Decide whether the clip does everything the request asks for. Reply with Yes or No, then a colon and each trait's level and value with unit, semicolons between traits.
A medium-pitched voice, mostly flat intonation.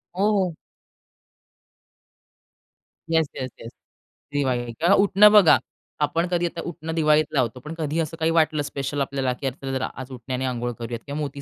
No: medium, 145 Hz; average, 3.9 semitones